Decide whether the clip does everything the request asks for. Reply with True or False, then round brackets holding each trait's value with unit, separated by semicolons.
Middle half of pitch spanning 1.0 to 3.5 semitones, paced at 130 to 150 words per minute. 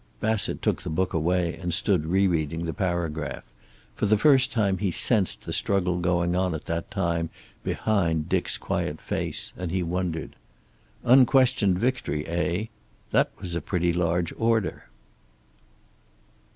True (3.1 semitones; 140 wpm)